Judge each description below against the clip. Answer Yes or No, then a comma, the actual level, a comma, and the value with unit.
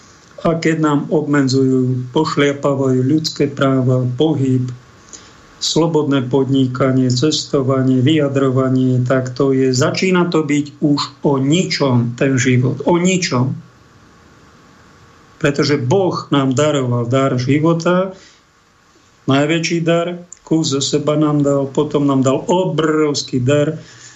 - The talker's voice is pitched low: No, medium, 145 Hz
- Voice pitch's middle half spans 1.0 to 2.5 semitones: No, average, 2.9 semitones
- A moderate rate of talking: No, slow, 105 wpm